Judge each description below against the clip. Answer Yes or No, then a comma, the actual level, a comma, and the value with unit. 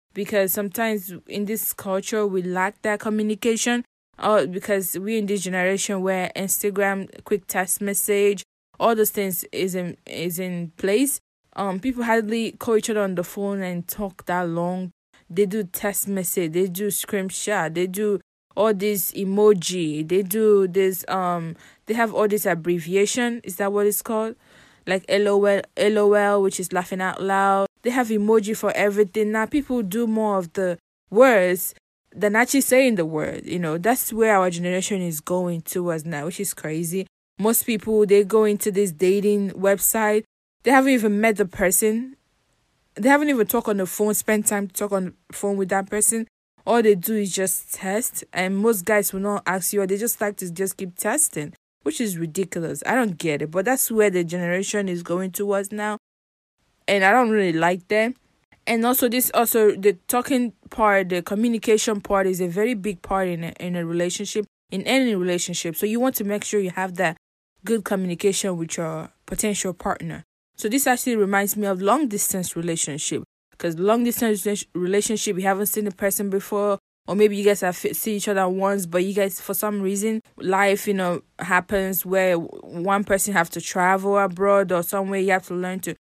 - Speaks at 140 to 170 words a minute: No, average, 185 wpm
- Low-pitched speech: No, high, 200 Hz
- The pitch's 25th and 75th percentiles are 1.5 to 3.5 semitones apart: Yes, narrow, 2.5 semitones